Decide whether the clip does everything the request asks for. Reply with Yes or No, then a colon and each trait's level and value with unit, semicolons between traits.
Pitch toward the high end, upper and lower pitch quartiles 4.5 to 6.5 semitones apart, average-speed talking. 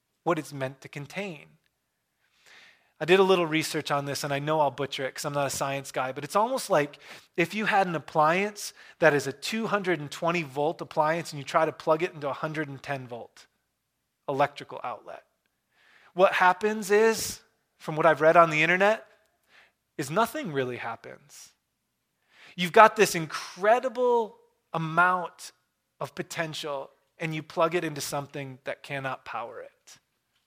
No: medium, 160 Hz; average, 4.8 semitones; average, 160 wpm